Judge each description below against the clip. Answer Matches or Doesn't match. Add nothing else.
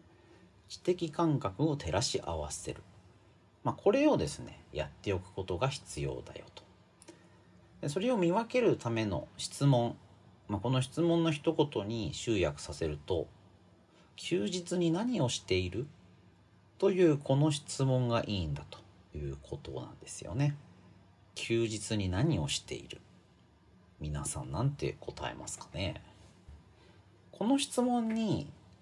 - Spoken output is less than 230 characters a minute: Doesn't match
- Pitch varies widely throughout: Matches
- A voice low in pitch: Matches